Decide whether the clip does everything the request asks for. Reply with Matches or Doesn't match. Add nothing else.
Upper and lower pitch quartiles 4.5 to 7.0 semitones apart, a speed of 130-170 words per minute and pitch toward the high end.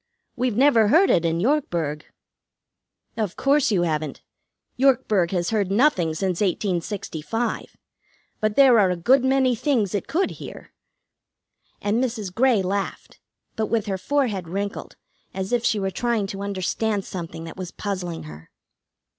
Matches